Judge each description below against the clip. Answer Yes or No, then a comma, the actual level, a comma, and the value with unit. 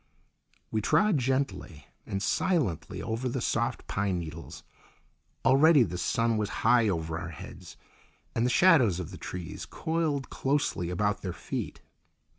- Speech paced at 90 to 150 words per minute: Yes, average, 140 wpm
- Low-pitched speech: Yes, low, 110 Hz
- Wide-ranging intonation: Yes, wide, 7.3 semitones